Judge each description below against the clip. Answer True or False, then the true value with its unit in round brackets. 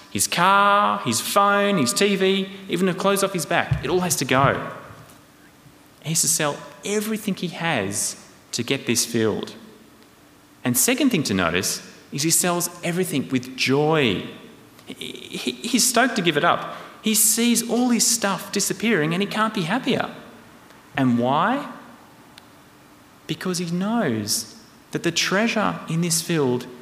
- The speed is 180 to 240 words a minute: False (150 wpm)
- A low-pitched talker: False (180 Hz)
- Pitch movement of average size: False (7.0 semitones)